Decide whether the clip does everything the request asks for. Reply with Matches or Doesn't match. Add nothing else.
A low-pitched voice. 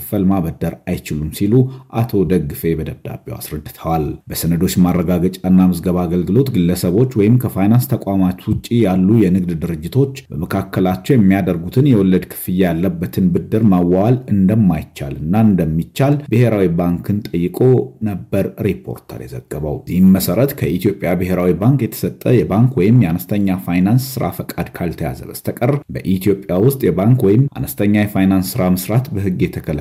Matches